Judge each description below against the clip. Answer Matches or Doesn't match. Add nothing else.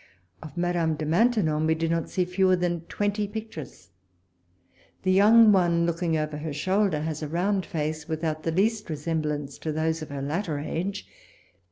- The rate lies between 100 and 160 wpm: Doesn't match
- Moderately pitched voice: Matches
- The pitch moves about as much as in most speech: Matches